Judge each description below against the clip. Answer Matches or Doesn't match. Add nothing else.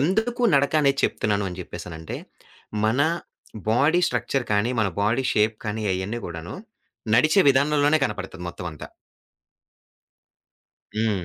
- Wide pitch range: Matches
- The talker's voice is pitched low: Matches